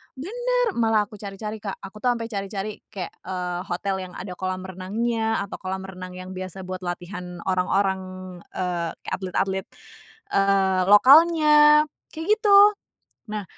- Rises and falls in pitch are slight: No, average, 3.7 semitones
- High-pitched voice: Yes, high, 195 Hz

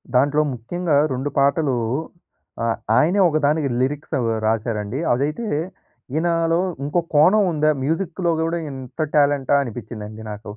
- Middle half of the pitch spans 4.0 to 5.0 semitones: Yes, average, 4.6 semitones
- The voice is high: No, medium, 145 Hz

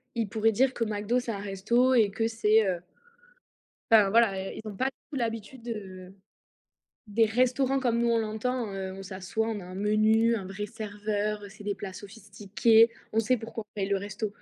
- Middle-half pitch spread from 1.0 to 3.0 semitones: Yes, narrow, 2.4 semitones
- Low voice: No, high, 215 Hz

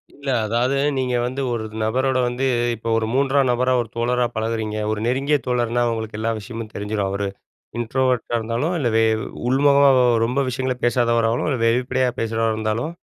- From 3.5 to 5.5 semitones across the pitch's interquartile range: No, narrow, 2.5 semitones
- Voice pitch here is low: Yes, low, 120 Hz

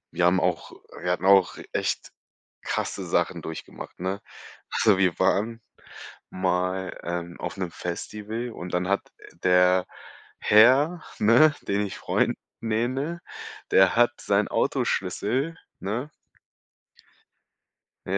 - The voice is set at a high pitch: No, low, 100 Hz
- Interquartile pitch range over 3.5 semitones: Yes, average, 4.3 semitones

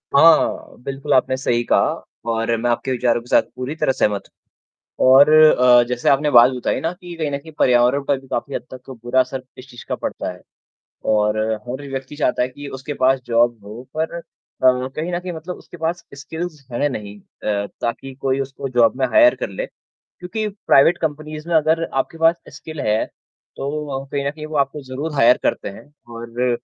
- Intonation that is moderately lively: Yes, average, 4.0 semitones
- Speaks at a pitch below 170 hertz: Yes, low, 135 Hz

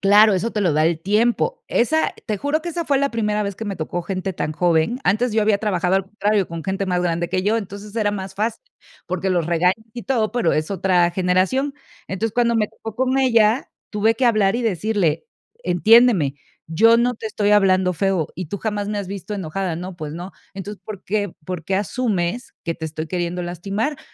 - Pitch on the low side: No, high, 200 Hz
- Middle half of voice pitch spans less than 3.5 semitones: No, average, 3.8 semitones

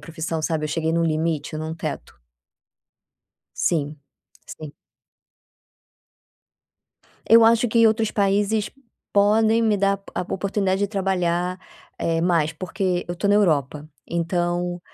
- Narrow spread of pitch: No, average, 3.8 semitones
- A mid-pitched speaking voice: Yes, medium, 180 Hz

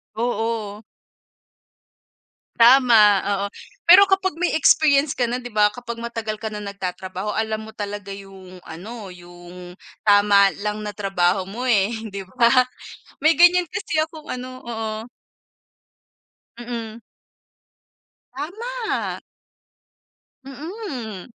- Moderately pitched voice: No, high, 225 Hz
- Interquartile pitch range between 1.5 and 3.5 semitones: No, average, 4.8 semitones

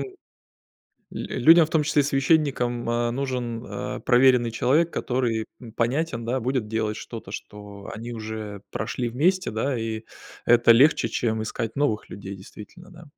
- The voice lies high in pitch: No, low, 120 Hz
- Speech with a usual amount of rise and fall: Yes, average, 3.7 semitones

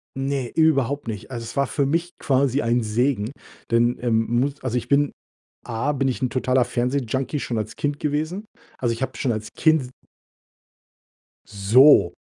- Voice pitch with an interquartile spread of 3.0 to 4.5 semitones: Yes, average, 3.3 semitones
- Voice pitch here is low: Yes, low, 130 Hz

